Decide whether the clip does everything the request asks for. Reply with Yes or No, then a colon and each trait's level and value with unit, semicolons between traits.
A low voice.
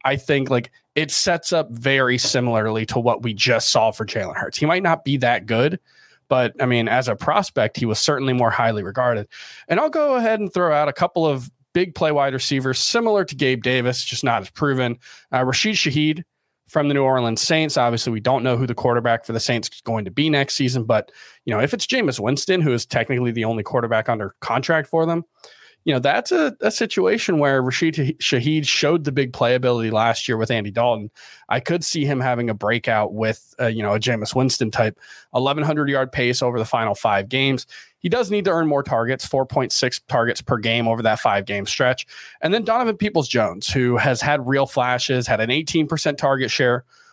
Yes: low, 130 Hz